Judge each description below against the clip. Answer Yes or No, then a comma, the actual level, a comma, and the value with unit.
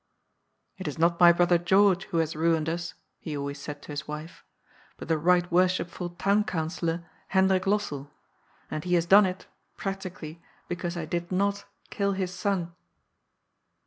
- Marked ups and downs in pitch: No, average, 2.7 semitones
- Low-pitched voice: No, medium, 175 Hz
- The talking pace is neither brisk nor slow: Yes, average, 170 wpm